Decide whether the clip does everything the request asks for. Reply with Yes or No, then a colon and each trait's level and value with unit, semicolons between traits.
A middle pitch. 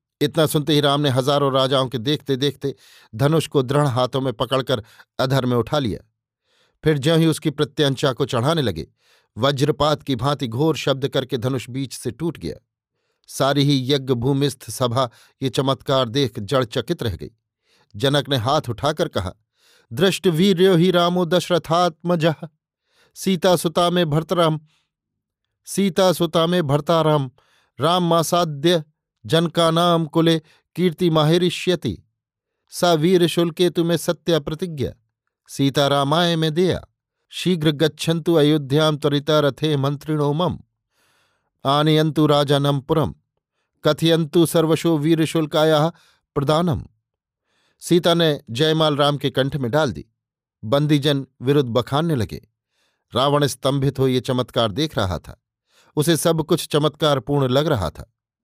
Yes: medium, 145 Hz